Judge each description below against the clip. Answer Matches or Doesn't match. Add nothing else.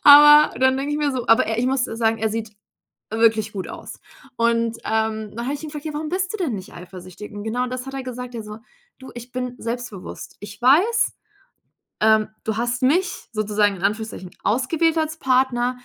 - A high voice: Matches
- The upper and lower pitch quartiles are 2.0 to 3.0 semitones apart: Doesn't match